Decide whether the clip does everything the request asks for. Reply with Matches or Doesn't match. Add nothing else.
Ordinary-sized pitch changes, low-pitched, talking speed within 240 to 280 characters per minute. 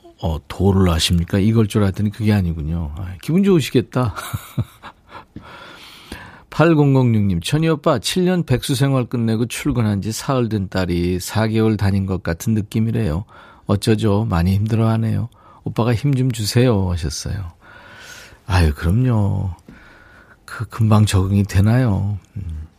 Matches